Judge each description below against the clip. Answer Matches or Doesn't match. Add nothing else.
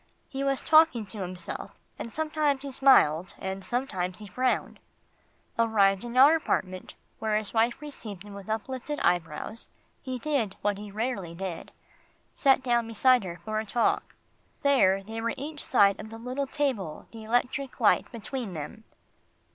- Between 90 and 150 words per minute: Doesn't match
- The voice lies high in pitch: Matches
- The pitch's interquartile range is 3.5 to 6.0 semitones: Matches